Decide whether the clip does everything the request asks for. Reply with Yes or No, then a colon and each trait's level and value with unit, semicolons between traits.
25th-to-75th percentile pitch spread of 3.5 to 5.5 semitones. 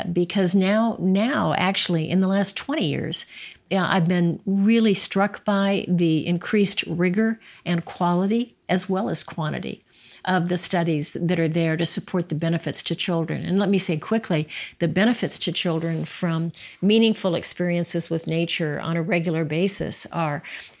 No: average, 2.8 semitones